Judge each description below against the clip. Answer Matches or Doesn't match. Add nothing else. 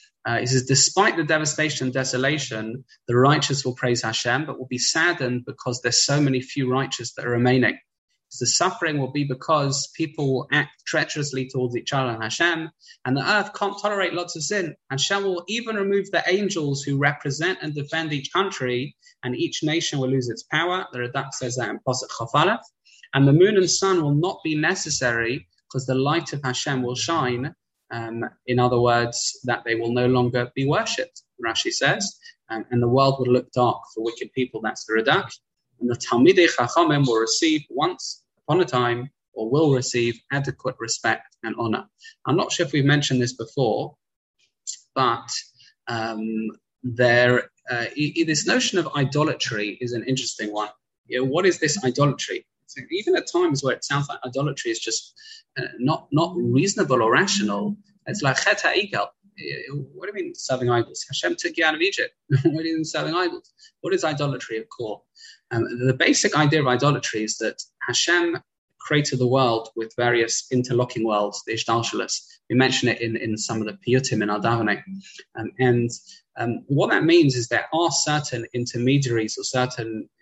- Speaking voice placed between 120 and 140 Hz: Matches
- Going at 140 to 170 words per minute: Doesn't match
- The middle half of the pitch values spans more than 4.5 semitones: Matches